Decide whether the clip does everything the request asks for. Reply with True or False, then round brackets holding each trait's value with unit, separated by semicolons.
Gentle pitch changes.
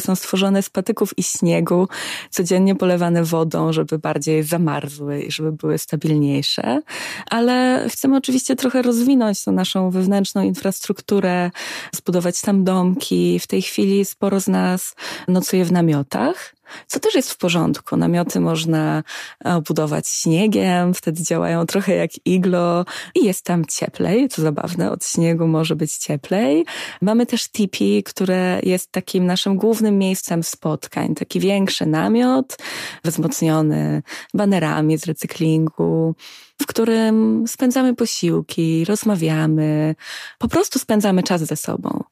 False (4.6 semitones)